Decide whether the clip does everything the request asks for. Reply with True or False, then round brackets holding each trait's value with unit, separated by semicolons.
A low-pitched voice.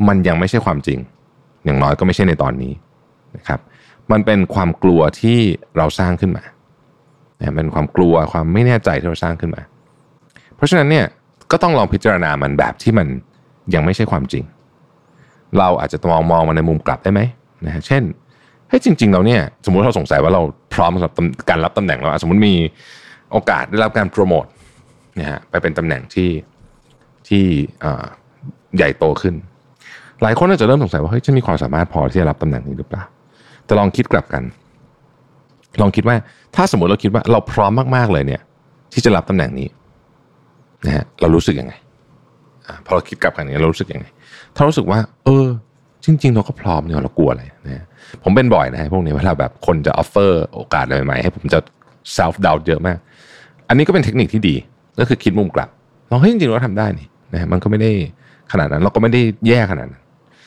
True (100 Hz)